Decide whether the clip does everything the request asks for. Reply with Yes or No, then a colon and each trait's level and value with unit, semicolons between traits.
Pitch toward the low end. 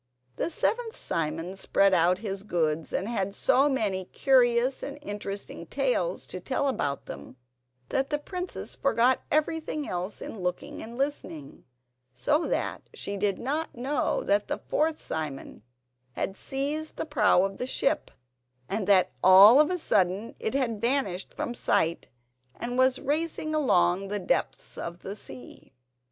No: high, 225 Hz